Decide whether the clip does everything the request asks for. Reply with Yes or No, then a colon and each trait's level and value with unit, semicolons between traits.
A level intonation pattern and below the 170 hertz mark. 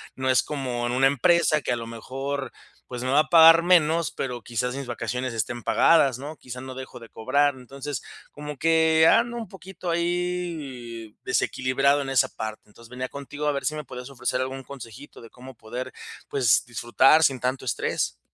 No: average, 3.5 semitones; low, 135 Hz